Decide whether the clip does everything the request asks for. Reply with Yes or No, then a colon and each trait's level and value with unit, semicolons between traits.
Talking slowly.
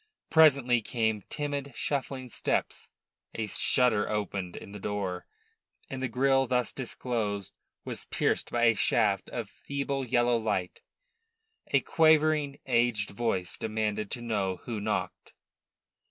Yes: slow, 125 wpm